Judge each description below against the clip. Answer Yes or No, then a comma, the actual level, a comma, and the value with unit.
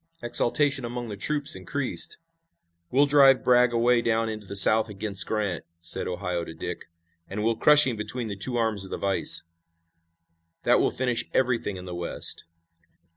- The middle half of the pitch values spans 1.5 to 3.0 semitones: No, average, 4.0 semitones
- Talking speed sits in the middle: Yes, average, 170 wpm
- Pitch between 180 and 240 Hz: No, low, 115 Hz